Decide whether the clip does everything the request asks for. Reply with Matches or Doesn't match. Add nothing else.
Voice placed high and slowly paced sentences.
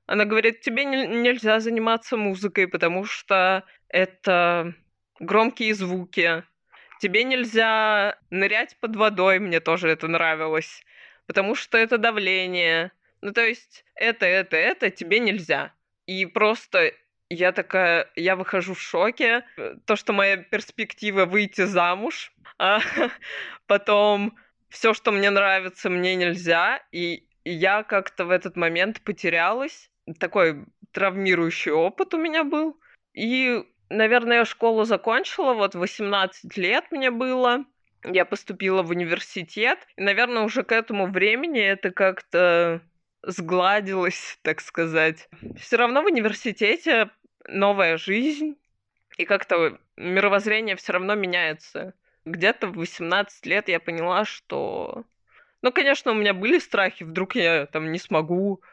Doesn't match